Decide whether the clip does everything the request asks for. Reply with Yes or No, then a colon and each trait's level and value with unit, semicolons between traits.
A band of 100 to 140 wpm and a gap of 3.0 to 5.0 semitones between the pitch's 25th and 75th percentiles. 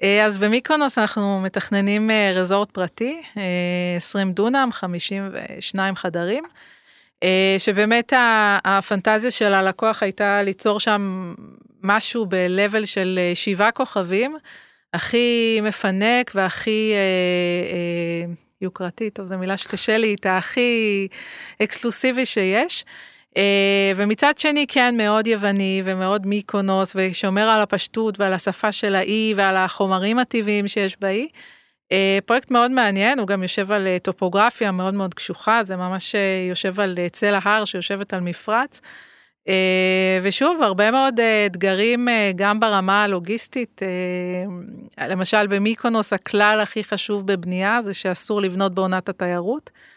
No: average, 120 wpm; narrow, 2.5 semitones